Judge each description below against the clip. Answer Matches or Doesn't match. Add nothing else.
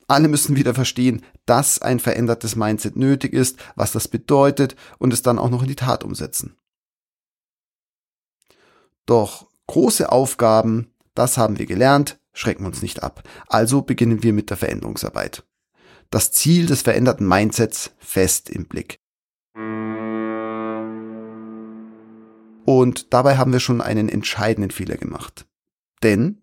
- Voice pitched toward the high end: Doesn't match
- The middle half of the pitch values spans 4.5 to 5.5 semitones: Doesn't match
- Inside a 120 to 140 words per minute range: Matches